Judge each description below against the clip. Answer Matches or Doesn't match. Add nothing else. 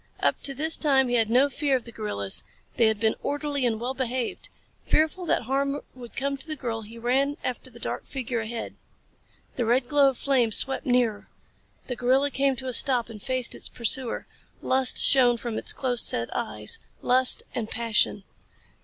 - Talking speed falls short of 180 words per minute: Doesn't match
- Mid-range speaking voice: Doesn't match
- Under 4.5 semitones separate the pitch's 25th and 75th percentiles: Matches